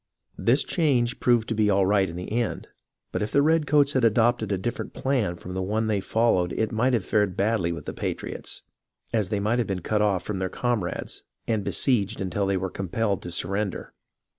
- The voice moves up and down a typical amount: Yes, average, 3.8 semitones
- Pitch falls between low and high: No, low, 105 Hz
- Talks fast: Yes, fast, 215 wpm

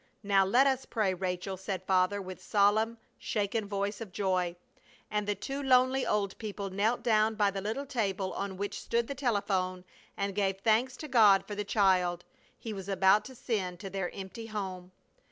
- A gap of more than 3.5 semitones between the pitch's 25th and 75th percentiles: No, average, 2.7 semitones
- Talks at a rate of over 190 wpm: No, average, 185 wpm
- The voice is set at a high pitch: Yes, high, 200 Hz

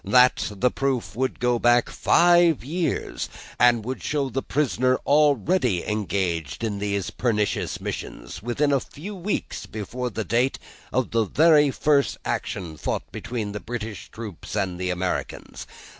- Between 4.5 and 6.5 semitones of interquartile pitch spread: Yes, average, 5.1 semitones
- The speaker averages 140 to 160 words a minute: Yes, average, 145 wpm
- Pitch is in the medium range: No, low, 120 Hz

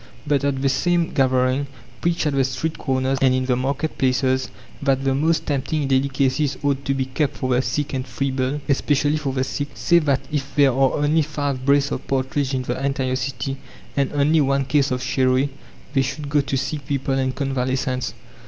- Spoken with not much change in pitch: Yes, narrow, 1.6 semitones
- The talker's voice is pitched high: No, low, 135 Hz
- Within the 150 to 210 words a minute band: Yes, average, 200 wpm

